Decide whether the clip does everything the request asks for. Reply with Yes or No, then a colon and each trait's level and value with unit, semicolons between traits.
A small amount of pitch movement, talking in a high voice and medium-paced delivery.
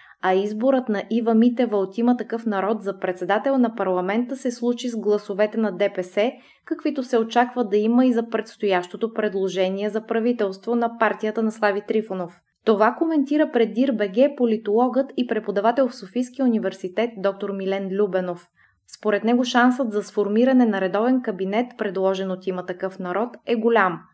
No: average, 3.6 semitones; high, 220 Hz; average, 155 wpm